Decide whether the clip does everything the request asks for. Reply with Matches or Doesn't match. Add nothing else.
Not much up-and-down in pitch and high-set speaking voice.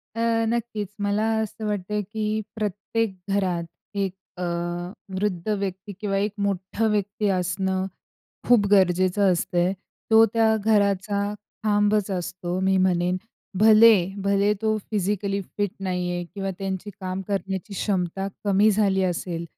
Matches